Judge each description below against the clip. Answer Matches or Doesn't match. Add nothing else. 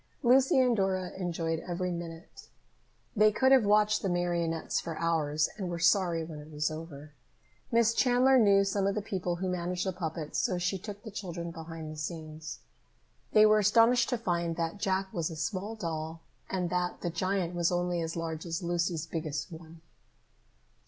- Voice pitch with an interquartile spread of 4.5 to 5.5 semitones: Doesn't match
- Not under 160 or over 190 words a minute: Matches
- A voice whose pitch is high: Doesn't match